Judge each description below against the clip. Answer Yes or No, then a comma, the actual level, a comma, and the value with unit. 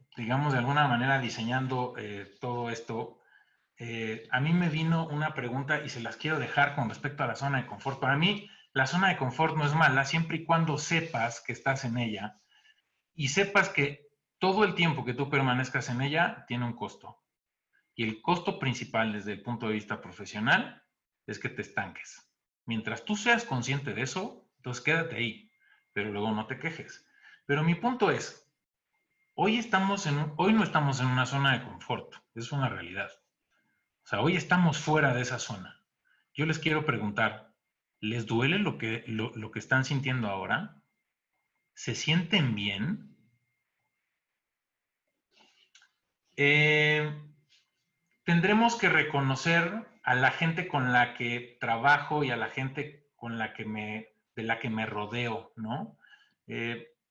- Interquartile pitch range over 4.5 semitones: Yes, wide, 5.6 semitones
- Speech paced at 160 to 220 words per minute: Yes, average, 165 wpm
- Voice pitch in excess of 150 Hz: No, low, 135 Hz